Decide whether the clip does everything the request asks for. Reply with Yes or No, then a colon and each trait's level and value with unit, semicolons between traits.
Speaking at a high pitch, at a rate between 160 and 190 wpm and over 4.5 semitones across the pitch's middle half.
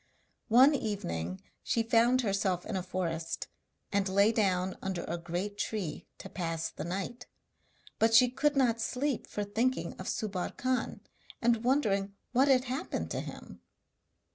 No: high, 210 Hz; average, 150 wpm; average, 5.0 semitones